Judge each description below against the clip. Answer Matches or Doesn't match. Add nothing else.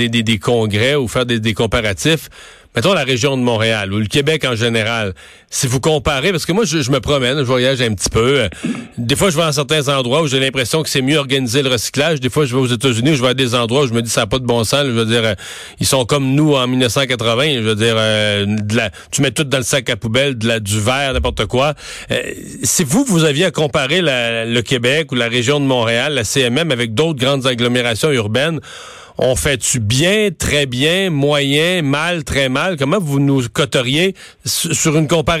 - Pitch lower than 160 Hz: Matches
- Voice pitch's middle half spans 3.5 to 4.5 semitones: Matches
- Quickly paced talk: Matches